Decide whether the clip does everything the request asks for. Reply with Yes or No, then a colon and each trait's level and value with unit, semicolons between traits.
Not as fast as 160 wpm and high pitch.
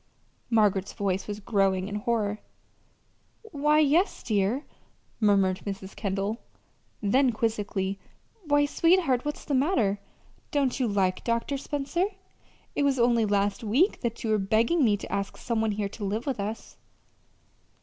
Yes: average, 145 wpm; high, 220 Hz